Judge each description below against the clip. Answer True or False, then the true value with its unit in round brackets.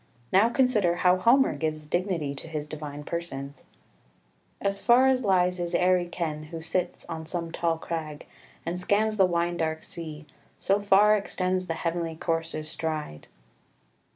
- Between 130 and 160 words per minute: True (155 wpm)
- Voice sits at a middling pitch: True (170 Hz)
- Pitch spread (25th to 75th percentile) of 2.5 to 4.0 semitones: True (2.9 semitones)